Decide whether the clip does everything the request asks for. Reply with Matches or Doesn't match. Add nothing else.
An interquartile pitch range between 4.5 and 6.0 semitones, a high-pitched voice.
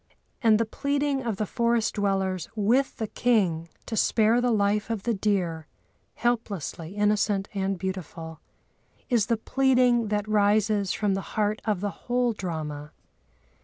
Doesn't match